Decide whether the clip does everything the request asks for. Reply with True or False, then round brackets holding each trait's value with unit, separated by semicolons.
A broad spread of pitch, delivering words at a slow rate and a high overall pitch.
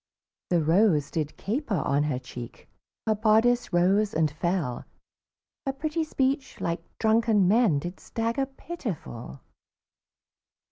True (7.2 semitones; 120 wpm; 200 Hz)